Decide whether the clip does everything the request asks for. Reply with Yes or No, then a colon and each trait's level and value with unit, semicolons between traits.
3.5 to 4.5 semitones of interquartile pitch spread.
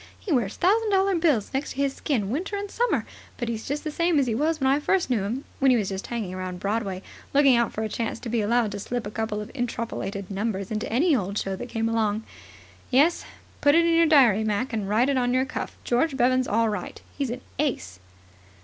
No: average, 5.2 semitones